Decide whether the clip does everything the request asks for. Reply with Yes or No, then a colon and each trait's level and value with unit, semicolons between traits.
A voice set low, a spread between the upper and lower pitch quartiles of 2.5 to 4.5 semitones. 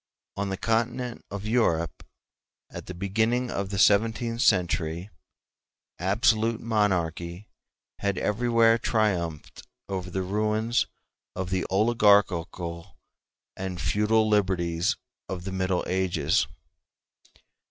Yes: low, 100 Hz; average, 3.6 semitones